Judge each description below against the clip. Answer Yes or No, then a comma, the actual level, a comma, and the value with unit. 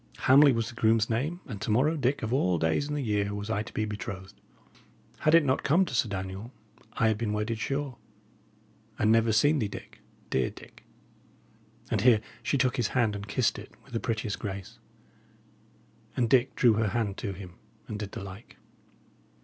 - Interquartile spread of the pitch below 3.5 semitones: No, average, 3.9 semitones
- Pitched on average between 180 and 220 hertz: No, low, 110 Hz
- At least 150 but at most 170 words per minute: No, average, 195 wpm